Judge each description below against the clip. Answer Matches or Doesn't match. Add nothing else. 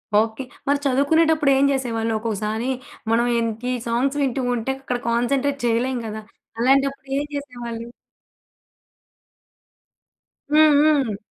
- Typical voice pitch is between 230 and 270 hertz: Matches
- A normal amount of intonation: Matches